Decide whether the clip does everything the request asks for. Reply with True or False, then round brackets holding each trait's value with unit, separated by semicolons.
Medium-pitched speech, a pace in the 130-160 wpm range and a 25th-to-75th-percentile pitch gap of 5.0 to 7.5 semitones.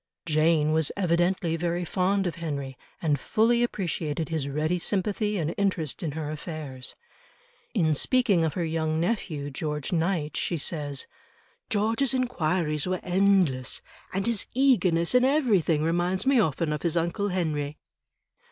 False (170 Hz; 145 wpm; 4.2 semitones)